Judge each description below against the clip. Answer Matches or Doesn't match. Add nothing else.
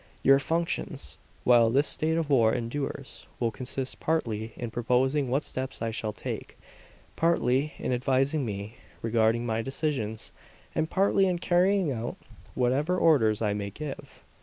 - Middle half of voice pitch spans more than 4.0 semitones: Matches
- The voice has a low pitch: Matches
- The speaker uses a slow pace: Doesn't match